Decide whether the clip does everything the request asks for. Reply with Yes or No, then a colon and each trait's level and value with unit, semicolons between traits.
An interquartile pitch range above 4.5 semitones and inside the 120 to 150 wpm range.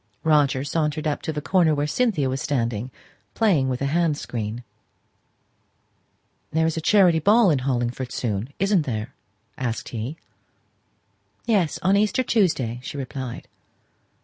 Yes: average, 5.2 semitones; average, 140 wpm